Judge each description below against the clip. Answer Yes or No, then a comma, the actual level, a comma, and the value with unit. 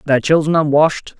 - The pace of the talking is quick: No, average, 150 wpm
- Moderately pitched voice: Yes, medium, 150 Hz